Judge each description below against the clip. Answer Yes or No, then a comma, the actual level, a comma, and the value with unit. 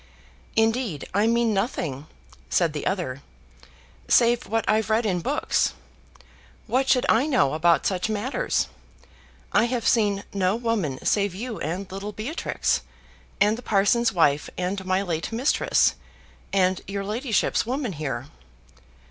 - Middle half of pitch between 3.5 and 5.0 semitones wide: Yes, average, 4.3 semitones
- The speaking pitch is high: Yes, high, 205 Hz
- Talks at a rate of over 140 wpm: No, slow, 135 wpm